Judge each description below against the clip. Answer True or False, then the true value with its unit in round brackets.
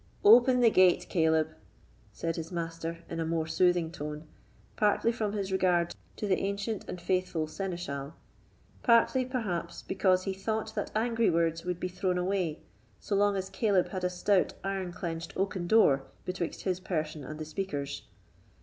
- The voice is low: False (180 Hz)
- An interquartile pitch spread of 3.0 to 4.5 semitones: True (3.3 semitones)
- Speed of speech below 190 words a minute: True (165 wpm)